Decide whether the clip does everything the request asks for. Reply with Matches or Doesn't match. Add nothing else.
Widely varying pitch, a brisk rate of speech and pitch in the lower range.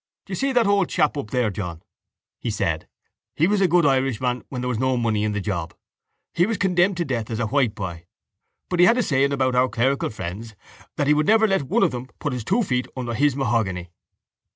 Matches